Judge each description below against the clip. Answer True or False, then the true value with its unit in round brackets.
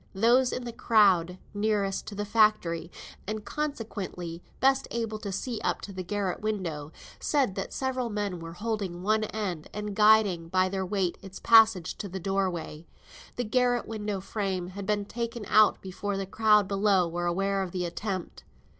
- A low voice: False (200 Hz)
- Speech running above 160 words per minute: True (170 wpm)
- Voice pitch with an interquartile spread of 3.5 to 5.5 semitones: False (2.9 semitones)